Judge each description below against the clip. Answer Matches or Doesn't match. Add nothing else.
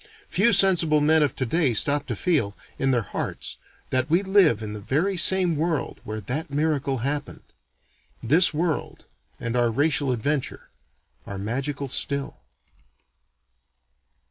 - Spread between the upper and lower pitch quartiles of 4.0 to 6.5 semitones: Matches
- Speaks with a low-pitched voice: Doesn't match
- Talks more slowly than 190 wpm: Matches